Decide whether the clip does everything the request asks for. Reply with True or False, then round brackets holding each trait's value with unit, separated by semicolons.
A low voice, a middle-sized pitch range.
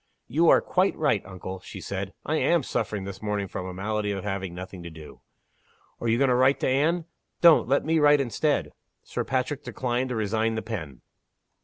False (110 Hz; 6.2 semitones)